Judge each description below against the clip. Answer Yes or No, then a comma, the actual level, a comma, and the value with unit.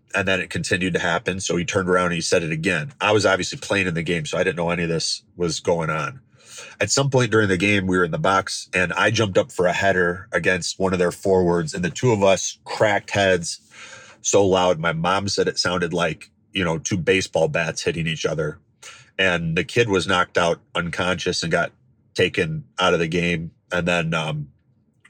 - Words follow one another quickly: Yes, fast, 225 wpm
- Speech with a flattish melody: Yes, narrow, 1.9 semitones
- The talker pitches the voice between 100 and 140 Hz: No, very low, 90 Hz